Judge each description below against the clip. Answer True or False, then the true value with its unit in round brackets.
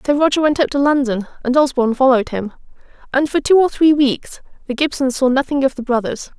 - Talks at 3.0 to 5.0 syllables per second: False (6.1 syllables/s)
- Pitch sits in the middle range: False (270 Hz)